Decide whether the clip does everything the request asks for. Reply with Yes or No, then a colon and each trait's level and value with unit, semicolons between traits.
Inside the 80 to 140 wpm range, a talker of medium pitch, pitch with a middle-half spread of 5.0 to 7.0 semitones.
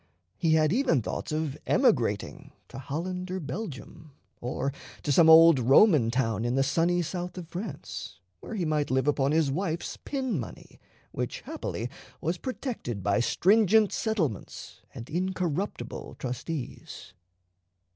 Yes: slow, 135 wpm; medium, 160 Hz; wide, 5.4 semitones